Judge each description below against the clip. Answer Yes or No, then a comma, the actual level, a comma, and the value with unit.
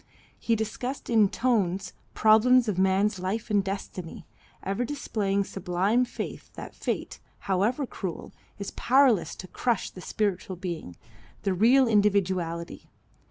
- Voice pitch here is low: No, high, 205 Hz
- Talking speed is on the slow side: Yes, slow, 125 wpm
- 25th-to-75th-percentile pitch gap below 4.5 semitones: Yes, average, 3.6 semitones